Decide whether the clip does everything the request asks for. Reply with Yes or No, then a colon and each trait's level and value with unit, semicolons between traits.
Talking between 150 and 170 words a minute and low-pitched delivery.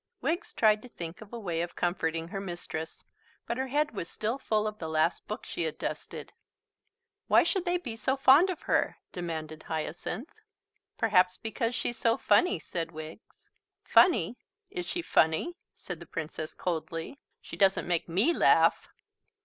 No: average, 165 wpm; high, 195 Hz